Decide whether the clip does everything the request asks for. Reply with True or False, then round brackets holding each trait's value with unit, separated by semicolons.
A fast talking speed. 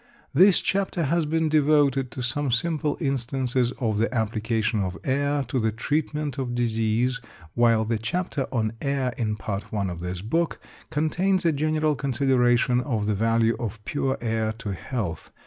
False (165 wpm)